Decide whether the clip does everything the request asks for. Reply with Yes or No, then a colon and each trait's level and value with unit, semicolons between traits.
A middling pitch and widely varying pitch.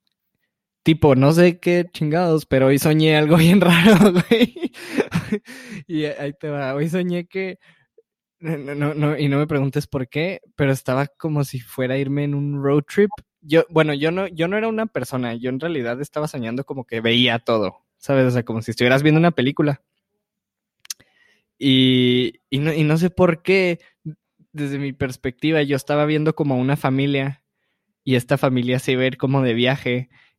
No: medium, 145 Hz; average, 4.3 semitones